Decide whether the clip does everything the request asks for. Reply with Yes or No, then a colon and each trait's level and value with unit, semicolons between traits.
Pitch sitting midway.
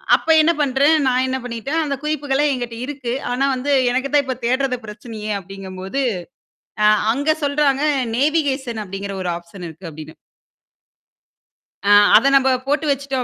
No: very high, 260 Hz